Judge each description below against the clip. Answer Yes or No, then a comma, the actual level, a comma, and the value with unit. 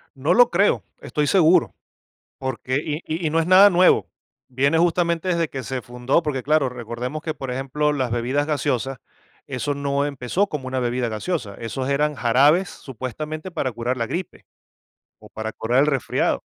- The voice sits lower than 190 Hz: Yes, medium, 140 Hz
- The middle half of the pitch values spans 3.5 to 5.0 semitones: Yes, average, 3.8 semitones